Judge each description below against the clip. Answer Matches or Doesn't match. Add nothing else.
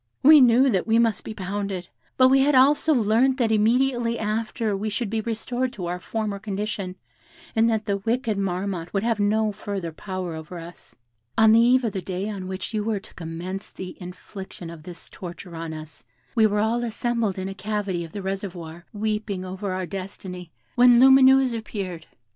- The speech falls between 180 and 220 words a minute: Matches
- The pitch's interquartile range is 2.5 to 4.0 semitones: Matches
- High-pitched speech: Matches